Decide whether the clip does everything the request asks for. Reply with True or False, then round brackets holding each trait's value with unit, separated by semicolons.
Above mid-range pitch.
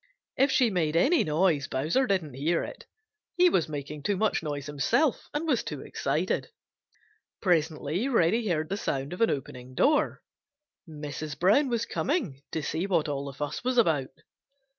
False (165 Hz)